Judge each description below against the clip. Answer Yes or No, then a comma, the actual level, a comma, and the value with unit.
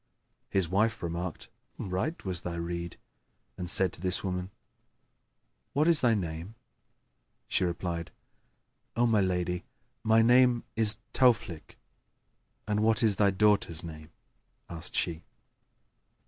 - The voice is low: Yes, very low, 95 Hz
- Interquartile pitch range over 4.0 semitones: Yes, average, 4.4 semitones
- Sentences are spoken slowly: Yes, slow, 120 wpm